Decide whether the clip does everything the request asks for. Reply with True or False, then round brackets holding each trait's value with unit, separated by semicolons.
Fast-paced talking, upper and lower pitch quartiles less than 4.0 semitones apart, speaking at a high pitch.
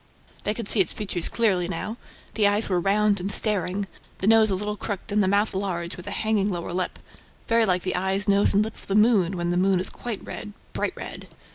True (235 wpm; 2.4 semitones; 200 Hz)